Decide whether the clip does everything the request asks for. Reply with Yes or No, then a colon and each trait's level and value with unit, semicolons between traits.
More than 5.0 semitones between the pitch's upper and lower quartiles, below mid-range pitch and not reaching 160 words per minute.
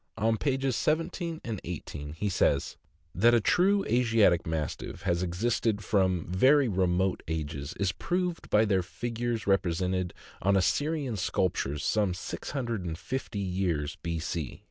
Yes: wide, 5.4 semitones; low, 100 Hz; slow, 135 wpm